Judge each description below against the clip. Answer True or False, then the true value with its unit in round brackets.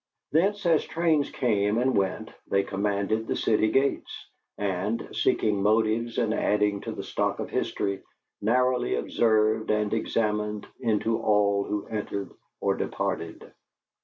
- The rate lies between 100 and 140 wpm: True (135 wpm)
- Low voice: True (110 Hz)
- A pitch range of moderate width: False (2.3 semitones)